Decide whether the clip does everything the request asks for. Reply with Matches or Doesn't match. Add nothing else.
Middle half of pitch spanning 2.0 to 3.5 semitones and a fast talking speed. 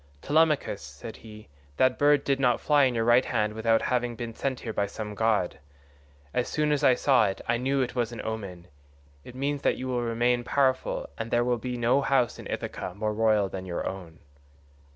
Matches